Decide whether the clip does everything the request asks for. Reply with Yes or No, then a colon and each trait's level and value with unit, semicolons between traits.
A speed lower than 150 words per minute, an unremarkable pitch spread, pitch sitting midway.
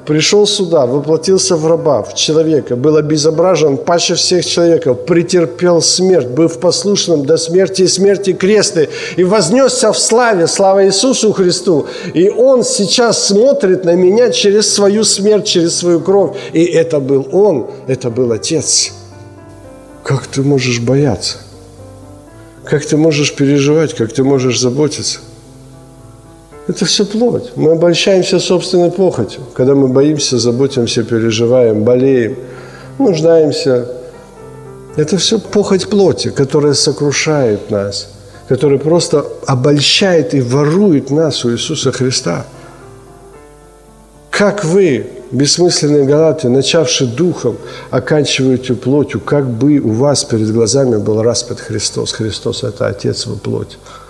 No: average, 125 wpm; wide, 6.1 semitones; medium, 150 Hz